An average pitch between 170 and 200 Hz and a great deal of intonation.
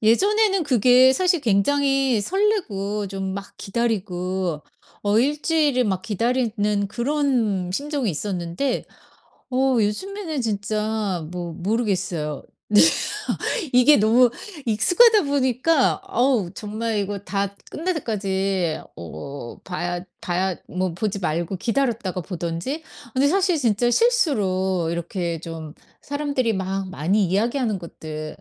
No: high, 210 Hz; wide, 6.1 semitones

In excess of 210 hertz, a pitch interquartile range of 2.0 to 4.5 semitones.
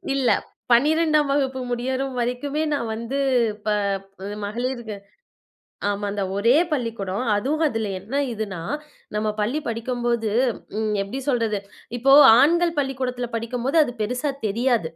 Yes: high, 245 Hz; average, 3.6 semitones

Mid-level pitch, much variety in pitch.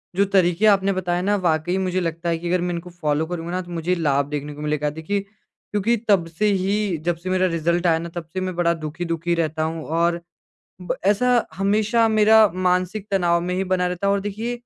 No: medium, 180 Hz; average, 2.9 semitones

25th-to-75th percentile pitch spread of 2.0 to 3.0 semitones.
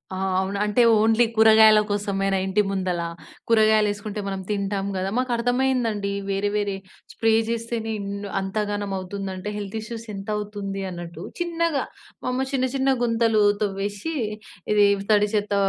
Yes: narrow, 2.4 semitones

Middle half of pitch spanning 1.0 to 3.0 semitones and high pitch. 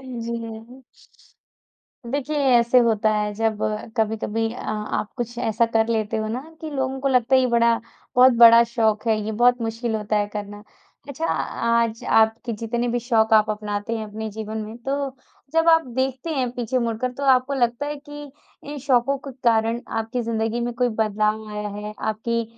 Yes: narrow, 2.5 semitones; high, 230 Hz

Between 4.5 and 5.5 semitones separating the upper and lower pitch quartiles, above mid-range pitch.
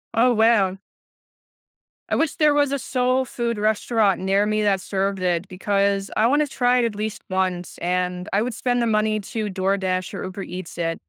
No: average, 4.0 semitones; high, 205 Hz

